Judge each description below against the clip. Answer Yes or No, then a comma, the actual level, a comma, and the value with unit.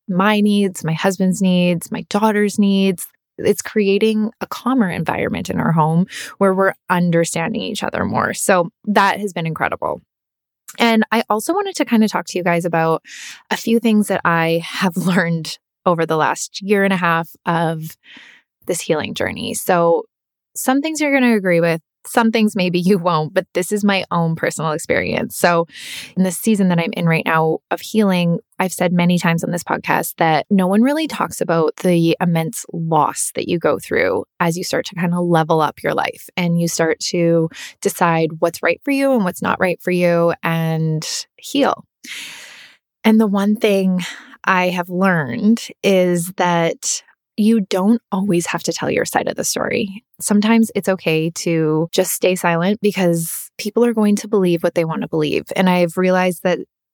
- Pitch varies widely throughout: No, average, 3.7 semitones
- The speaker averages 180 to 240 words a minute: Yes, average, 185 wpm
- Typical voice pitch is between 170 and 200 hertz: Yes, medium, 185 Hz